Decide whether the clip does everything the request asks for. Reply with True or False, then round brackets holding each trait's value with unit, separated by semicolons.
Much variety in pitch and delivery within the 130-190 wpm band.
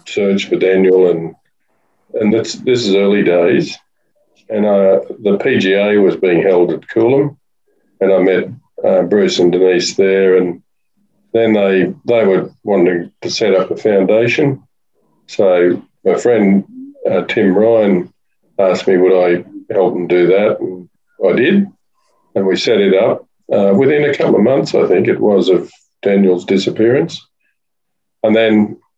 True (7.7 semitones; 155 wpm)